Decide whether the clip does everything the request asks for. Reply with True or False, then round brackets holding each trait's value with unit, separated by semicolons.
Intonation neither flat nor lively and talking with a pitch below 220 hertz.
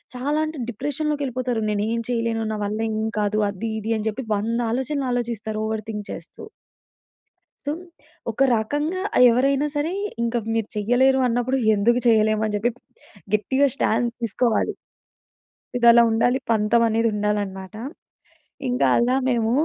False (3.0 semitones; 230 Hz)